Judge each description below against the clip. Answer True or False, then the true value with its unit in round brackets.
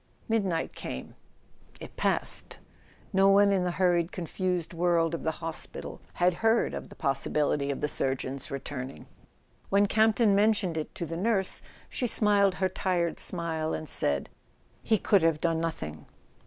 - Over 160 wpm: False (155 wpm)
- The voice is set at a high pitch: False (175 Hz)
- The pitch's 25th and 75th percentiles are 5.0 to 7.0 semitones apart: False (3.9 semitones)